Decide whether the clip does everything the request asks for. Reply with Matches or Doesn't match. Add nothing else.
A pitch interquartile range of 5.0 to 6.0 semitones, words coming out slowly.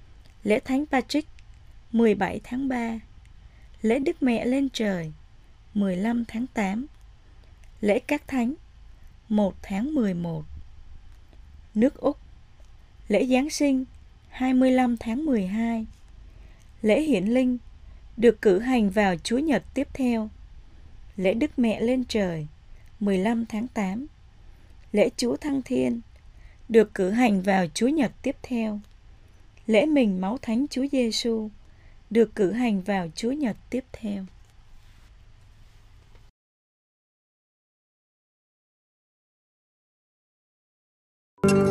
Matches